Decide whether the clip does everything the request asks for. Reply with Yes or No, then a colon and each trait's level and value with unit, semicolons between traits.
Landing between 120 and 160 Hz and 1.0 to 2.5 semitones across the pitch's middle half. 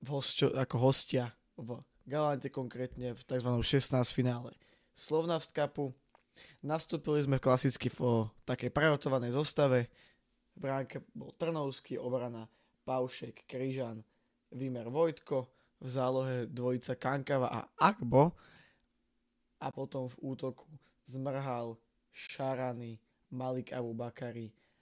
Yes: low, 130 Hz; narrow, 2.2 semitones